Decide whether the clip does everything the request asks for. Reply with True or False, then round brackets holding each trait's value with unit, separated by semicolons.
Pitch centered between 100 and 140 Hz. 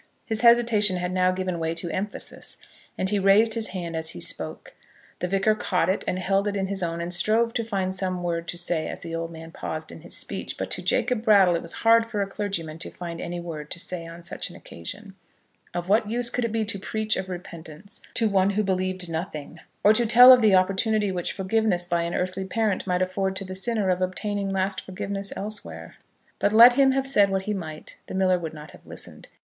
False (190 Hz)